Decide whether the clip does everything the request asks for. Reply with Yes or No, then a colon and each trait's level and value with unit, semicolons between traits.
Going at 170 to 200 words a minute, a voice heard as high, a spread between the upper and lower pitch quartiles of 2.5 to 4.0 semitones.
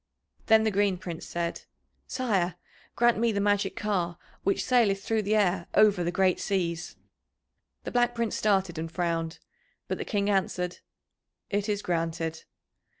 No: average, 150 wpm; high, 195 Hz; average, 3.4 semitones